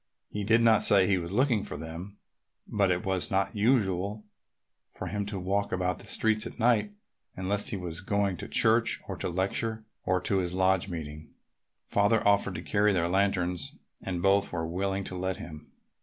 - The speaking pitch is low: Yes, very low, 95 Hz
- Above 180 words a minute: Yes, average, 190 wpm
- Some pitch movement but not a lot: No, narrow, 2.2 semitones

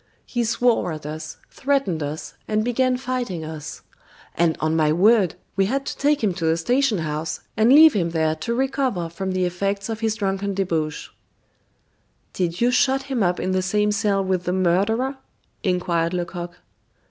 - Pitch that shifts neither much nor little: No, wide, 5.9 semitones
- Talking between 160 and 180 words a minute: Yes, average, 175 wpm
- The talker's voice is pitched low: No, high, 195 Hz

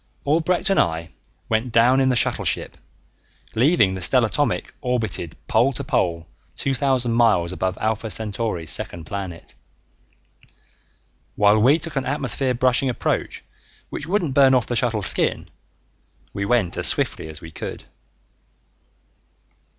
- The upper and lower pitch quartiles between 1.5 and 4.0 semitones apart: No, wide, 5.4 semitones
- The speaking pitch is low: Yes, low, 115 Hz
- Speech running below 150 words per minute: Yes, slow, 135 wpm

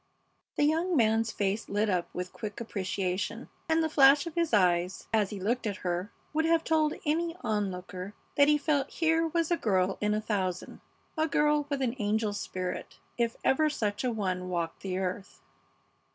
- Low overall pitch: No, high, 220 Hz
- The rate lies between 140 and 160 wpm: No, average, 185 wpm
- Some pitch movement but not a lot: No, wide, 7.8 semitones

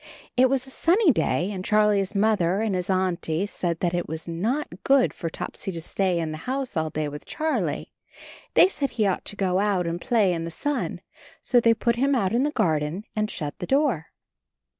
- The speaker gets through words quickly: Yes, fast, 210 wpm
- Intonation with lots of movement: Yes, wide, 6.3 semitones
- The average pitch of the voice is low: No, high, 195 Hz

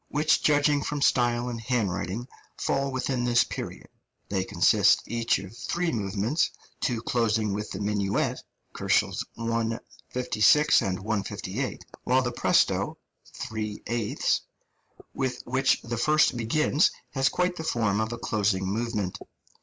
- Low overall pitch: Yes, low, 115 Hz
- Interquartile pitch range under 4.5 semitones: Yes, average, 3.8 semitones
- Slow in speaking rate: Yes, slow, 130 wpm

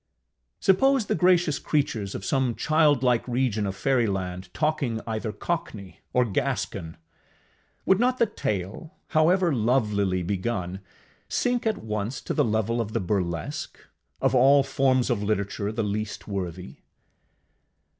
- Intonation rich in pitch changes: Yes, wide, 6.3 semitones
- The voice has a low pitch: Yes, low, 115 Hz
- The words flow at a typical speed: No, slow, 130 wpm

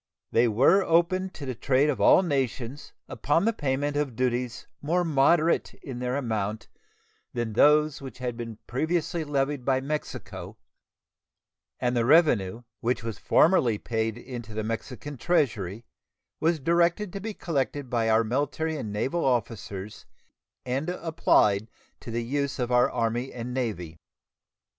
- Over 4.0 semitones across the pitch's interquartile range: Yes, average, 4.7 semitones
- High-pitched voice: No, low, 130 Hz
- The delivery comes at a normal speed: Yes, average, 145 wpm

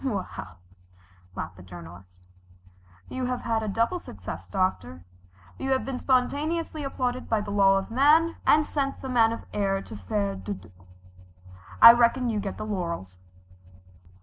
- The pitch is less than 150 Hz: No, high, 215 Hz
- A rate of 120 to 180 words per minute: Yes, average, 155 wpm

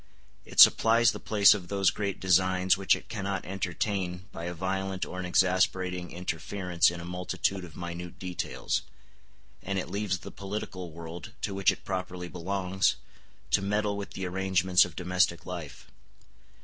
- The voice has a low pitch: Yes, very low, 95 Hz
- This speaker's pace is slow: No, average, 160 wpm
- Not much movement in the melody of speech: Yes, narrow, 1.6 semitones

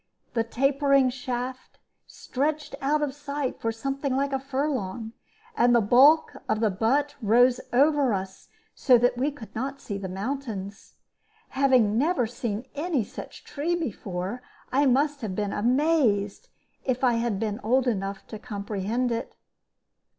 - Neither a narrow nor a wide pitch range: Yes, average, 4.2 semitones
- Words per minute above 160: No, average, 150 wpm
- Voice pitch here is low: No, very high, 250 Hz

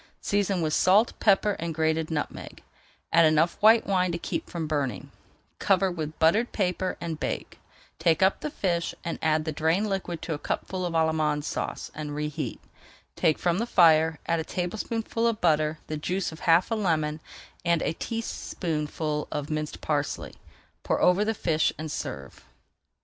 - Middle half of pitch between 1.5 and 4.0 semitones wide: Yes, average, 3.3 semitones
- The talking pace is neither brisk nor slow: Yes, average, 170 wpm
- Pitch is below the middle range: No, medium, 165 Hz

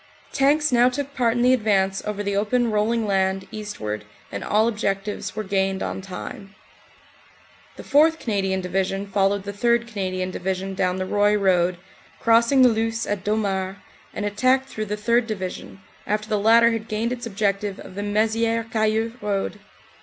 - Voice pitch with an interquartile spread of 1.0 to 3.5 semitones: Yes, average, 2.9 semitones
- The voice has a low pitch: No, high, 210 Hz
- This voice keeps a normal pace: Yes, average, 170 wpm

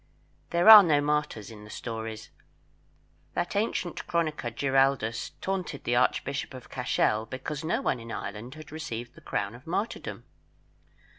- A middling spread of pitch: No, wide, 5.7 semitones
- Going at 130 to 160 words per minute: Yes, average, 145 wpm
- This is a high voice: No, low, 135 Hz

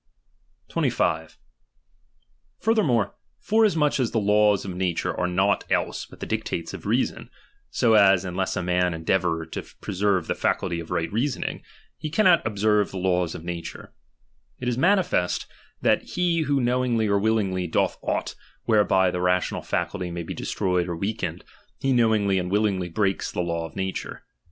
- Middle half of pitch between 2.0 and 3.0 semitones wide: No, average, 4.3 semitones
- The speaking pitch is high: No, very low, 95 Hz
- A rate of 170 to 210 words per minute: No, average, 160 wpm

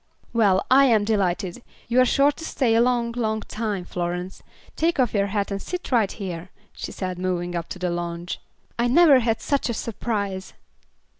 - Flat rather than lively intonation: No, average, 4.7 semitones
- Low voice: No, high, 215 Hz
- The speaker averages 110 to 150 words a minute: No, average, 190 wpm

